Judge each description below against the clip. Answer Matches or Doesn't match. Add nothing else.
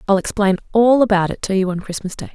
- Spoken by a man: Doesn't match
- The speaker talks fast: Matches